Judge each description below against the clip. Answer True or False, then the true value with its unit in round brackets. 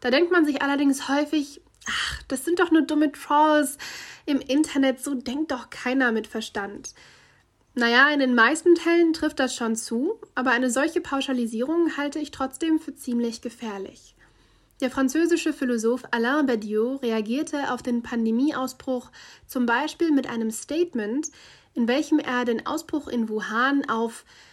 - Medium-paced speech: True (155 wpm)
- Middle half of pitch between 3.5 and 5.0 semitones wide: True (4.1 semitones)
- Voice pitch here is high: True (270 Hz)